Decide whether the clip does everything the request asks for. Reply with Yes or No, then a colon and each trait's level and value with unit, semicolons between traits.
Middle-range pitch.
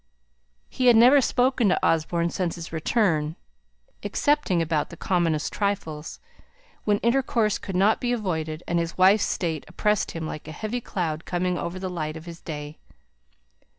Yes: medium, 175 Hz